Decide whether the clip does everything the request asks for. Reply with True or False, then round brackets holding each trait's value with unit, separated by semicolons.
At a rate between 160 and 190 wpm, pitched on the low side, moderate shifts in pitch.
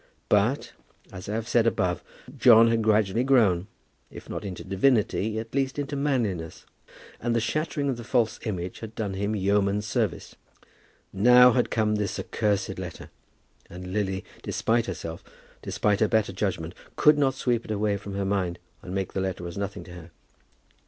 True (170 wpm; 105 Hz; 3.5 semitones)